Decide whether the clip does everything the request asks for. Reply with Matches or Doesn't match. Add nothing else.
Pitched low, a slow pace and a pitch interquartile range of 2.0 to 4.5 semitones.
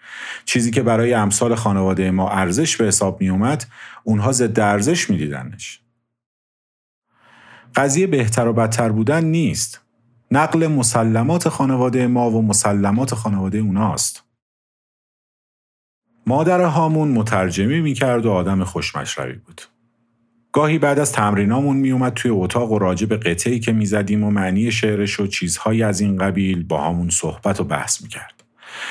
Doesn't match